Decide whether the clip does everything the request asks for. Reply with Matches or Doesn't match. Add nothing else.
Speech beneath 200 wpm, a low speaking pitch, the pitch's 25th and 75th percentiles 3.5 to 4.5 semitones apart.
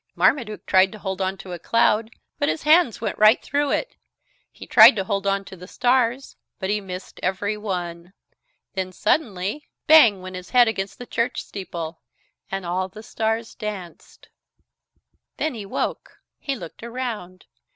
Doesn't match